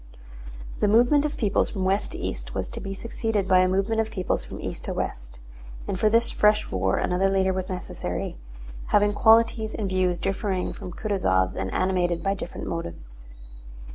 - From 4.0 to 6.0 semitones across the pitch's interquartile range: No, average, 3.0 semitones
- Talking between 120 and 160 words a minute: No, average, 180 wpm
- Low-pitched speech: No, high, 190 Hz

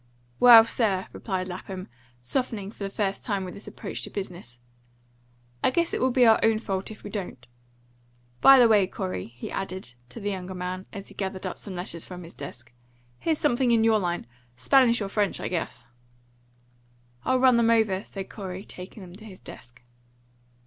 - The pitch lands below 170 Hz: No, high, 195 Hz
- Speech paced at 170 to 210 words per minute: Yes, average, 190 wpm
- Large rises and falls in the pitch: No, average, 3.6 semitones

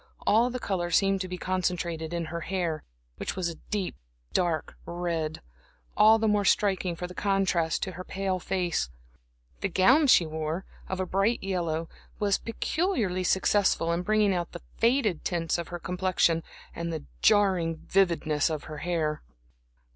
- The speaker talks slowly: No, average, 160 wpm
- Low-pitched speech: No, medium, 180 Hz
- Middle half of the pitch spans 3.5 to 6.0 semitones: No, average, 2.7 semitones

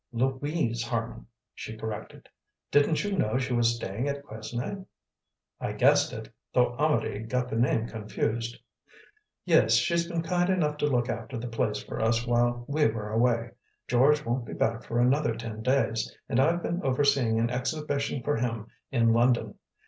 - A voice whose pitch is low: Yes, low, 120 Hz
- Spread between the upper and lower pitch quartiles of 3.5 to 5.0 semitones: Yes, average, 3.8 semitones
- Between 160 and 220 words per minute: Yes, average, 165 wpm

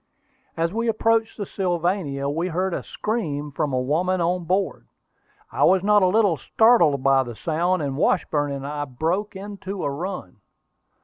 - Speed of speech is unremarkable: Yes, average, 170 wpm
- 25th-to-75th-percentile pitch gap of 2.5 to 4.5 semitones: No, average, 5.2 semitones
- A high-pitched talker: No, medium, 175 Hz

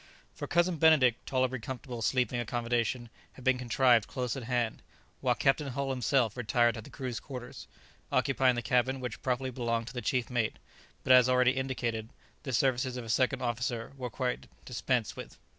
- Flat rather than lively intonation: Yes, narrow, 1.7 semitones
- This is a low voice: Yes, low, 125 Hz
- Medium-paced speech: Yes, average, 175 wpm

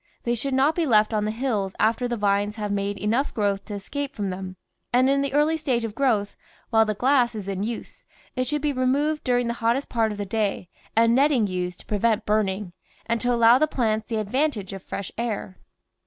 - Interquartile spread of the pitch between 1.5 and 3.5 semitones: No, average, 4.0 semitones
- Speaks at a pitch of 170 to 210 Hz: No, high, 225 Hz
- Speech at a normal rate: No, fast, 230 wpm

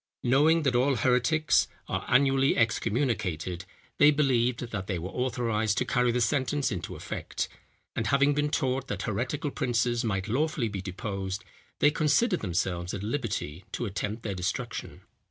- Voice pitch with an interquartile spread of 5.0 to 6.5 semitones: Yes, average, 5.3 semitones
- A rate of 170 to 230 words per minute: No, average, 155 wpm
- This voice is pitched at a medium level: No, low, 120 Hz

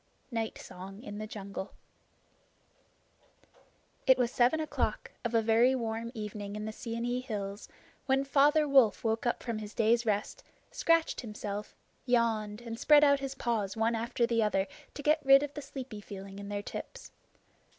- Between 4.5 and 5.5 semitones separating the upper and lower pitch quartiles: No, average, 3.8 semitones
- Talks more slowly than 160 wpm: No, average, 165 wpm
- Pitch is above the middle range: Yes, high, 230 Hz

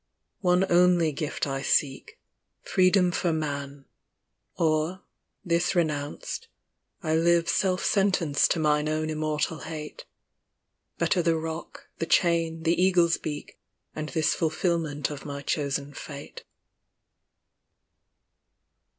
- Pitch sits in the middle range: Yes, medium, 160 Hz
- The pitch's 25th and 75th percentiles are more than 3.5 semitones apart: No, narrow, 2.5 semitones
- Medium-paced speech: No, slow, 110 wpm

